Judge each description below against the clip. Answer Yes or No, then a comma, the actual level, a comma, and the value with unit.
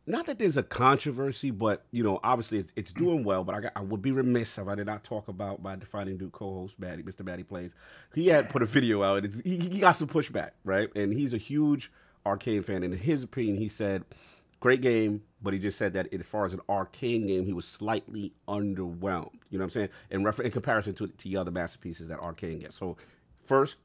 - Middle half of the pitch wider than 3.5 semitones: Yes, average, 4.1 semitones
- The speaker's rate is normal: No, fast, 240 wpm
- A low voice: Yes, low, 105 Hz